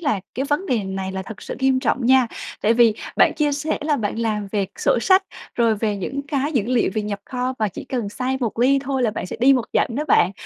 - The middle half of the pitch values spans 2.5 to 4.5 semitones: Yes, average, 4.2 semitones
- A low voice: No, high, 245 Hz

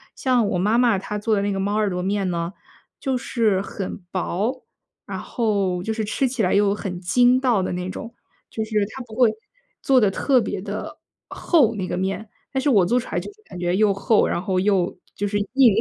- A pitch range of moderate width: Yes, average, 4.0 semitones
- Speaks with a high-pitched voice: Yes, high, 210 Hz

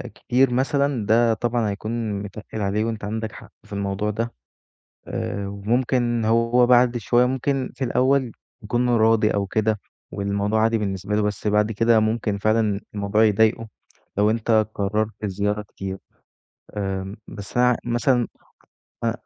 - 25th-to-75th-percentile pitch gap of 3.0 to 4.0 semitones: No, narrow, 2.6 semitones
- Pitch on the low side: Yes, low, 110 Hz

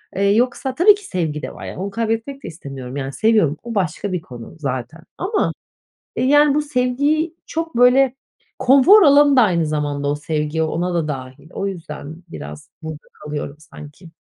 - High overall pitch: No, medium, 180 Hz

